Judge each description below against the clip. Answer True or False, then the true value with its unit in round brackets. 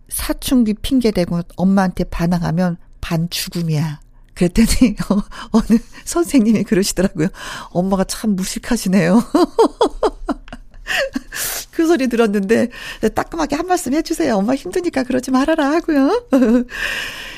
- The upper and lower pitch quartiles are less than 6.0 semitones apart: False (6.6 semitones)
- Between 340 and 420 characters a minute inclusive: False (275 characters per minute)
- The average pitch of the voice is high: True (230 Hz)